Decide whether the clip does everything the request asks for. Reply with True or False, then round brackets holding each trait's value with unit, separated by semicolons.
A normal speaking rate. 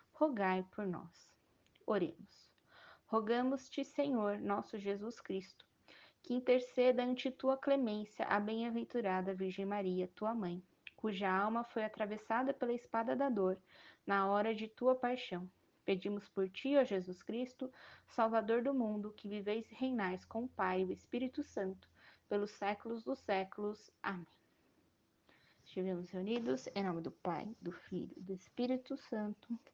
True (140 wpm)